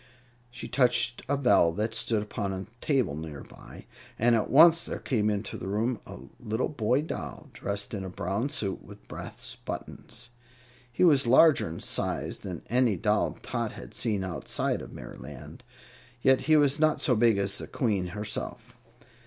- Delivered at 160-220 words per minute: Yes, average, 170 wpm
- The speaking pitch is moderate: No, low, 110 Hz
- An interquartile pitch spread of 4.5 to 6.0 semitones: Yes, average, 4.9 semitones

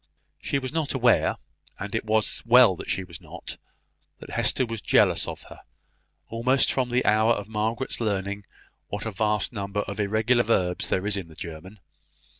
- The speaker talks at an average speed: Yes, average, 180 wpm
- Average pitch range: Yes, average, 3.1 semitones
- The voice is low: Yes, low, 105 Hz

